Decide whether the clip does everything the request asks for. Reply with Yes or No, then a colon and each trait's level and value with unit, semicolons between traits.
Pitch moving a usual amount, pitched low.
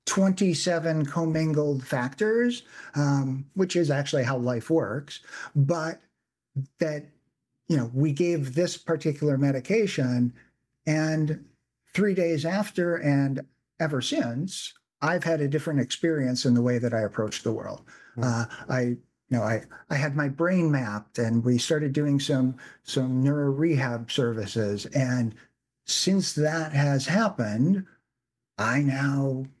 No: average, 4.3 semitones; medium, 145 Hz